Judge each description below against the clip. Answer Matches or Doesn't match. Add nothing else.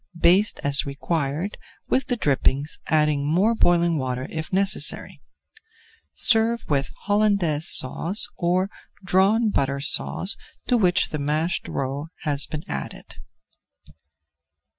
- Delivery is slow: Matches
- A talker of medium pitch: Matches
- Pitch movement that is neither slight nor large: Doesn't match